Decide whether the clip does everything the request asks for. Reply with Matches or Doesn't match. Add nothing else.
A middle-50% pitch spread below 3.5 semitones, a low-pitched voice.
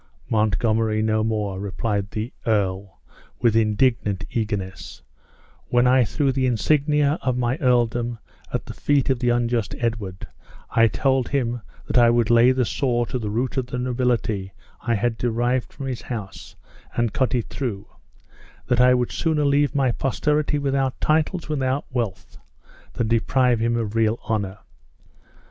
Matches